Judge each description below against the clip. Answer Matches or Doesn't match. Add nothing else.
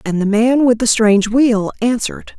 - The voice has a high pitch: Matches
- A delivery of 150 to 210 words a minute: Matches